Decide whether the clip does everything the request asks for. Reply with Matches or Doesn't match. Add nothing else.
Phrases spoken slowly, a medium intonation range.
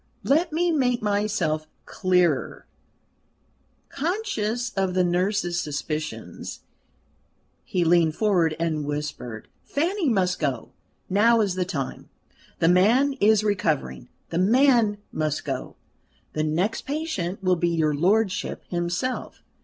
Doesn't match